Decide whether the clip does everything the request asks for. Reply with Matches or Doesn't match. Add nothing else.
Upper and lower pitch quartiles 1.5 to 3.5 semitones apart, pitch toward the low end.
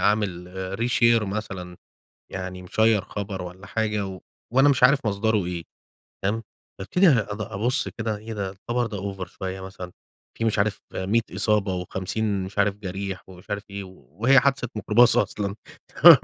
Matches